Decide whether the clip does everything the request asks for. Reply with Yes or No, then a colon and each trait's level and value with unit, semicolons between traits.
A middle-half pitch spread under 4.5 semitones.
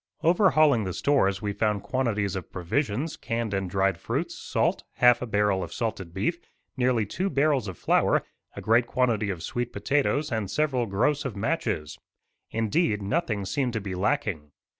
No: wide, 5.6 semitones